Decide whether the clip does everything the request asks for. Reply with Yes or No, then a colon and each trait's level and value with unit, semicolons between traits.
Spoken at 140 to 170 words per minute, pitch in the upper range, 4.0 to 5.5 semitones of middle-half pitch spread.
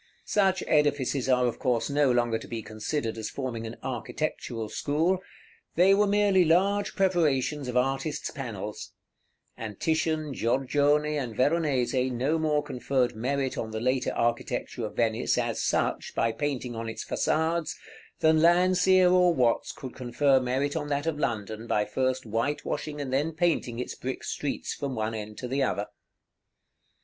No: average, 160 wpm; low, 135 Hz; average, 4.6 semitones